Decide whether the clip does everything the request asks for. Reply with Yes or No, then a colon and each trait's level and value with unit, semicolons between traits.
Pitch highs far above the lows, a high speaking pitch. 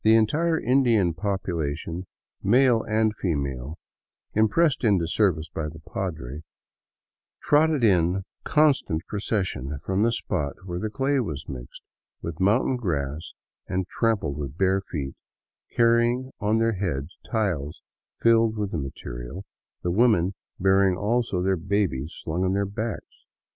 No: wide, 5.8 semitones; very low, 95 Hz